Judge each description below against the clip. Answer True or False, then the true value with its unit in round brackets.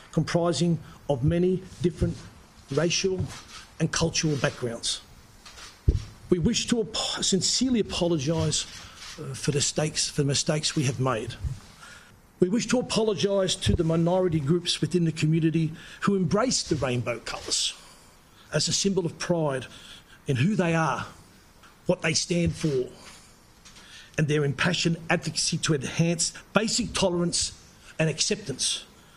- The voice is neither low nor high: True (165 Hz)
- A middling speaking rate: False (125 wpm)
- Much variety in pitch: False (3.9 semitones)